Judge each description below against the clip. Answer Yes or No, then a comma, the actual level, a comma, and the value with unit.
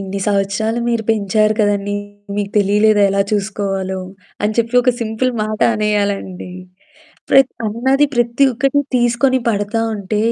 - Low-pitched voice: No, high, 215 Hz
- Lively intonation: No, average, 2.7 semitones